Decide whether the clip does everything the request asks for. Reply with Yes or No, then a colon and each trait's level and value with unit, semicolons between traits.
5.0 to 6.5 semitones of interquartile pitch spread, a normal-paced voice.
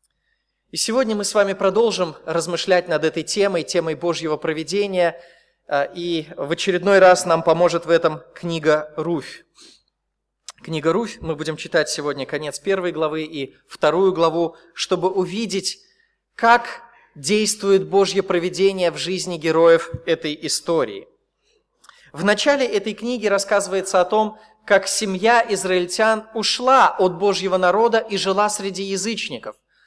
No: average, 4.1 semitones; average, 130 wpm